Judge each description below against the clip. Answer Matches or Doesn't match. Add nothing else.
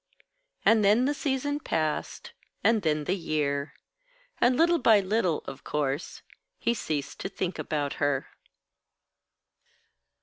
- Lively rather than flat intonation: Matches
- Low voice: Doesn't match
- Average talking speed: Doesn't match